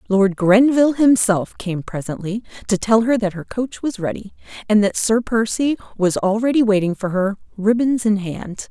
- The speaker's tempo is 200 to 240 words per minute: No, average, 165 wpm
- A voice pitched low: No, high, 210 Hz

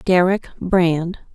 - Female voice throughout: Yes, female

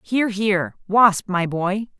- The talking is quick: No, average, 150 wpm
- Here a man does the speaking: No, female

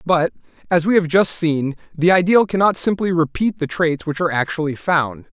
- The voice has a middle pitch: Yes, medium, 170 Hz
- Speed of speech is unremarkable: Yes, average, 190 wpm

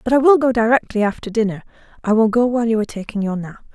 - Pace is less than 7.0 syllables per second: No, 7.3 syllables/s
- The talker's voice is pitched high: Yes, high, 225 Hz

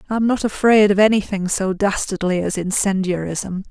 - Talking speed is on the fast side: No, average, 145 wpm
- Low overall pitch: No, high, 195 Hz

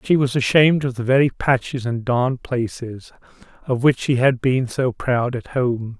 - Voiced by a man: Yes, male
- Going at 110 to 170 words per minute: No, average, 190 wpm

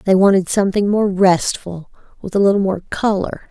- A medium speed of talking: Yes, average, 170 wpm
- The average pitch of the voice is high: Yes, high, 195 Hz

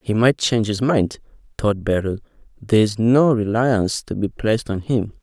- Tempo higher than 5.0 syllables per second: No, 4.9 syllables/s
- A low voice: Yes, low, 110 Hz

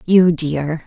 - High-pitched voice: No, medium, 160 Hz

